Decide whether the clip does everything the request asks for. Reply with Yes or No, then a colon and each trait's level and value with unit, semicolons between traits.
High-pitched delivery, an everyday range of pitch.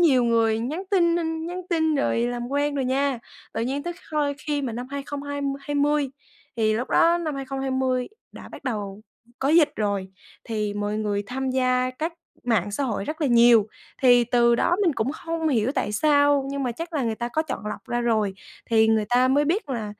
Yes: very high, 260 Hz; average, 3.9 semitones